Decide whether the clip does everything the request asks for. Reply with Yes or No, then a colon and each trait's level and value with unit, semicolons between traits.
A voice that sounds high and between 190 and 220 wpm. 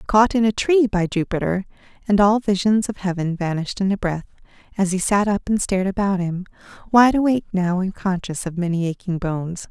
Yes: high, 195 Hz; average, 200 wpm